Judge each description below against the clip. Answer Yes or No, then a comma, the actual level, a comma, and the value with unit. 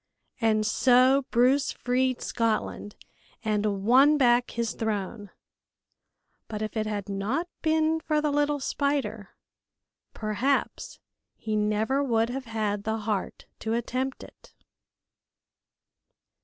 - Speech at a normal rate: No, slow, 115 wpm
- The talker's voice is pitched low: No, high, 235 Hz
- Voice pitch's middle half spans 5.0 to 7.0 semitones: No, average, 4.1 semitones